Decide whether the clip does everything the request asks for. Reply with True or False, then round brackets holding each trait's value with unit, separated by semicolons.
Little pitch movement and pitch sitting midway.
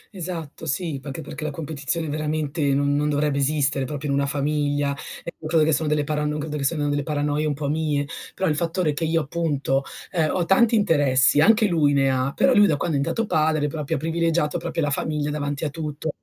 True (2.1 semitones; 150 Hz)